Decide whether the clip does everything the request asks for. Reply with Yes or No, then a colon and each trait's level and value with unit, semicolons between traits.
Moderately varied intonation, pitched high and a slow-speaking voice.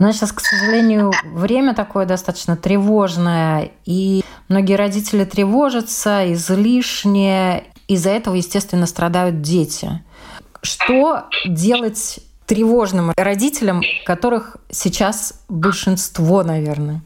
Yes: average, 3.3 semitones; high, 195 Hz; slow, 90 wpm